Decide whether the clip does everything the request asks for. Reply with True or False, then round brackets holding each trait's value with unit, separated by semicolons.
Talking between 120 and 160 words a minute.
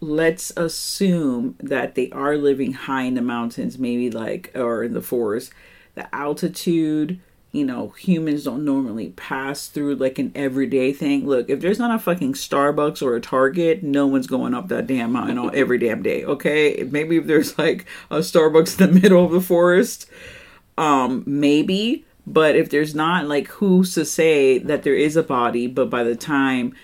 False (185 wpm)